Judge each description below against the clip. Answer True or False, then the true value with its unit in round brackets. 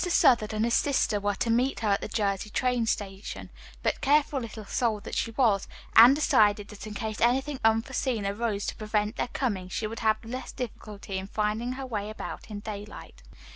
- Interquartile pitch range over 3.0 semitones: False (2.7 semitones)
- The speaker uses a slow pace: False (190 wpm)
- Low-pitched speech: False (220 Hz)